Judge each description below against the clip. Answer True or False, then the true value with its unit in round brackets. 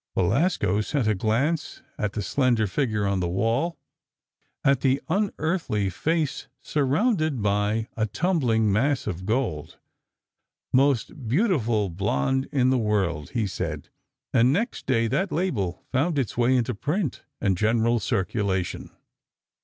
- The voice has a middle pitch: False (115 Hz)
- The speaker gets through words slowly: True (130 wpm)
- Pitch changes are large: True (5.8 semitones)